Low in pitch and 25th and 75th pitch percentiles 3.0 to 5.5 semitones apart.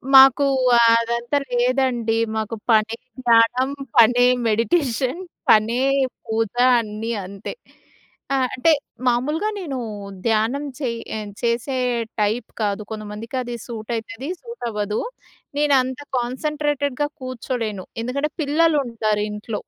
No: high, 235 Hz; average, 3.3 semitones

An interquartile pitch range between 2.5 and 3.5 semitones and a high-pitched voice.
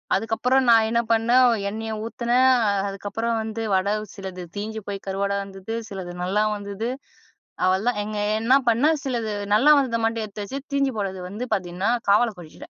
Yes: average, 3.0 semitones; high, 220 Hz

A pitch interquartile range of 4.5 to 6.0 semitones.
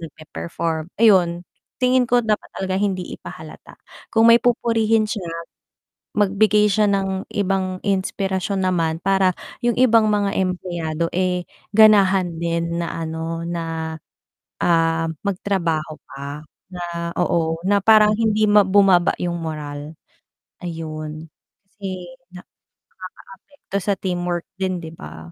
No: average, 3.6 semitones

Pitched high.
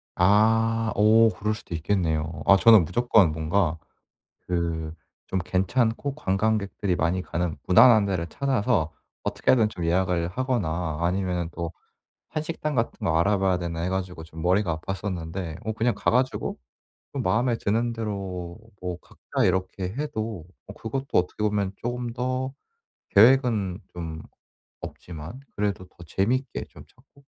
No: very low, 95 Hz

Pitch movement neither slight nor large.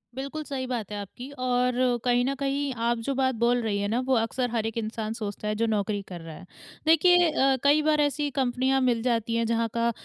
Yes: average, 3.3 semitones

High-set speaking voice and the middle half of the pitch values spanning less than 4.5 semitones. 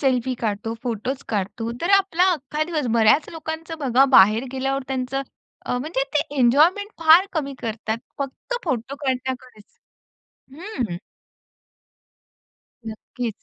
No: very high, 265 Hz; average, 4.8 semitones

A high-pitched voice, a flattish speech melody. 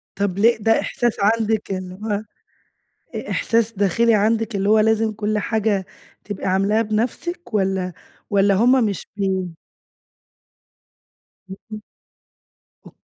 Yes: high, 210 Hz; narrow, 2.3 semitones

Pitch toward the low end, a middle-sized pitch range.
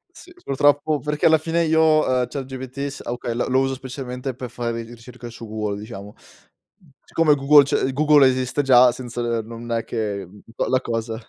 Yes: low, 130 Hz; average, 3.3 semitones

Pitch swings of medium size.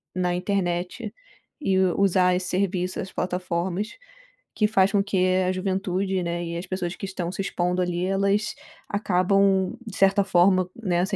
No: narrow, 1.7 semitones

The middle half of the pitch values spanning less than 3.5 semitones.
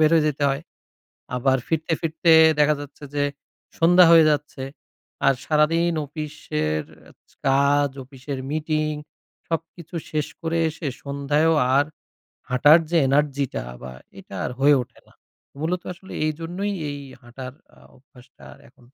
Yes: average, 2.9 semitones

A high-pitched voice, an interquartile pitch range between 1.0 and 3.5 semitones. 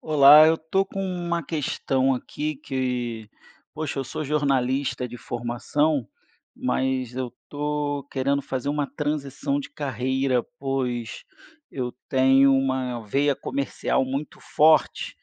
No: low, 135 Hz; narrow, 2.5 semitones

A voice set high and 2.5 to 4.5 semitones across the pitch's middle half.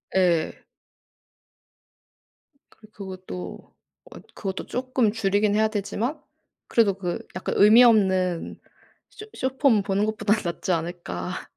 Yes: high, 200 Hz; average, 3.3 semitones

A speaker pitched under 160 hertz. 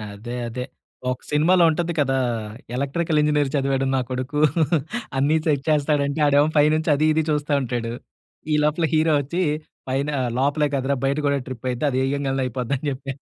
Yes: medium, 140 Hz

